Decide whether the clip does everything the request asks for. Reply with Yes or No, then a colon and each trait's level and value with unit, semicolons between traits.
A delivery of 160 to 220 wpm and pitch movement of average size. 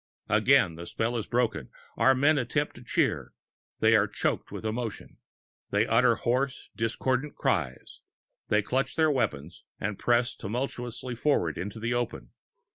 No: average, 145 wpm; average, 3.4 semitones